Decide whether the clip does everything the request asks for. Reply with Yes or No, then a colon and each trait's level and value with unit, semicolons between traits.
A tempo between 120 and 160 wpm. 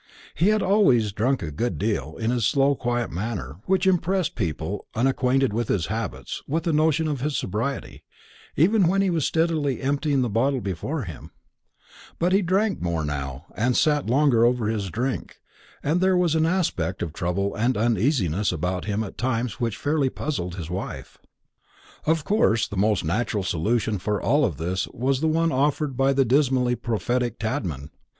No: average, 175 wpm